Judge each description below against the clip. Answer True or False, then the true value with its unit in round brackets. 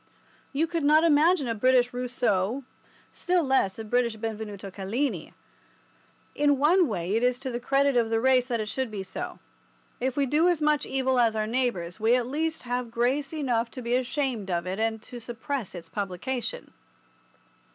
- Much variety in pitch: False (3.9 semitones)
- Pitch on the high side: True (245 Hz)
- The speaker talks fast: False (185 wpm)